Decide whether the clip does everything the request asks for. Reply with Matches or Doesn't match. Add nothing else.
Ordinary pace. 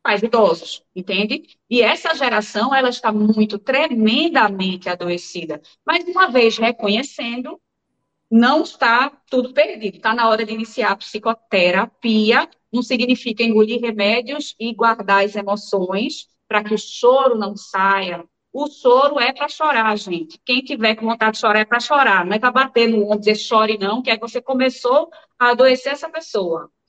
Matches